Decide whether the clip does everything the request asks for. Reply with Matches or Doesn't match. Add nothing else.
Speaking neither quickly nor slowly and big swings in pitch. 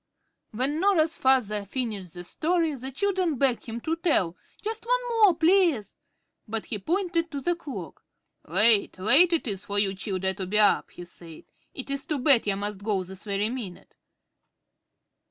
Matches